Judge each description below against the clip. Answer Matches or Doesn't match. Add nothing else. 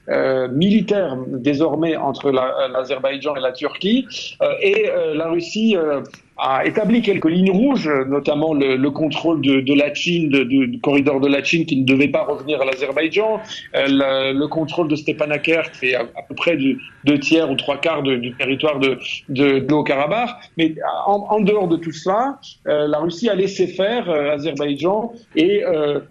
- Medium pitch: Matches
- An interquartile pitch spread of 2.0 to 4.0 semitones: Doesn't match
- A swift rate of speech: Matches